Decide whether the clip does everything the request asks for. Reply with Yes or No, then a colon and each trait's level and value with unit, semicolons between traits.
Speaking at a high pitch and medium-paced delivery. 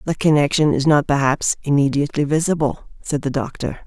No: medium, 140 Hz; average, 155 wpm